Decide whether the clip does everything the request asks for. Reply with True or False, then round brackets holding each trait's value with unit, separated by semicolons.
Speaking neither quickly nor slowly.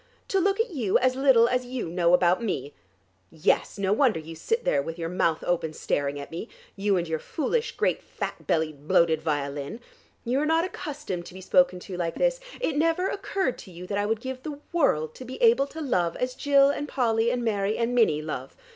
False (220 wpm)